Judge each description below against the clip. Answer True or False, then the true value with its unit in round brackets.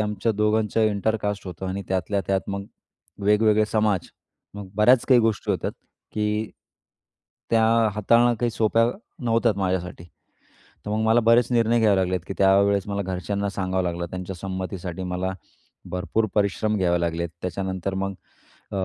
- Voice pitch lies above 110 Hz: False (100 Hz)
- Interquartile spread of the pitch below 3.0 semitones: True (2.6 semitones)